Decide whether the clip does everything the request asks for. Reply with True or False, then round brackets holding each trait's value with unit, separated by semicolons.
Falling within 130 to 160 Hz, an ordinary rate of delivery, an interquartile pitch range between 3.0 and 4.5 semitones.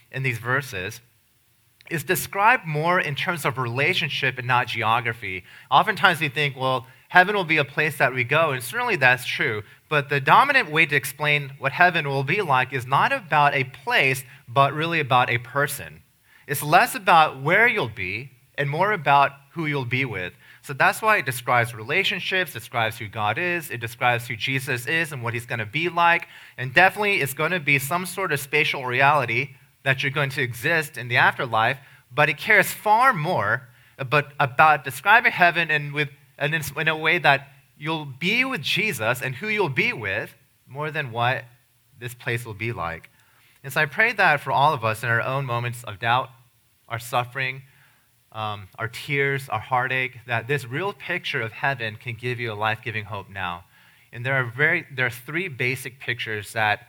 True (135 Hz; 190 wpm; 4.0 semitones)